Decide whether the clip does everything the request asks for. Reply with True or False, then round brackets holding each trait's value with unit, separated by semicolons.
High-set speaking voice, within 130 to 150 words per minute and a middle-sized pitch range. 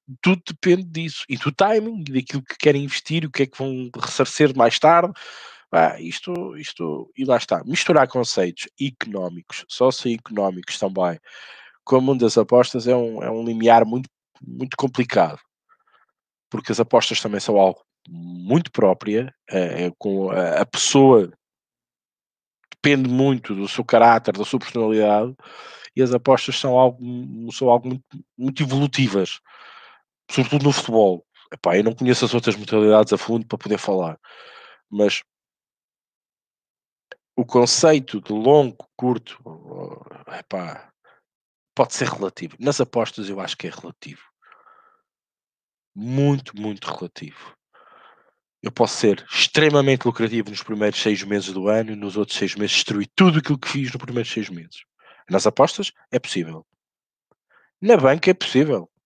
False (125 Hz; 145 wpm; 4.9 semitones)